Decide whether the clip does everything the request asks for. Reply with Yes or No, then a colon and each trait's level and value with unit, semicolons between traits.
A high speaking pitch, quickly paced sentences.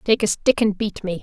Yes: high, 210 Hz; fast, 295 wpm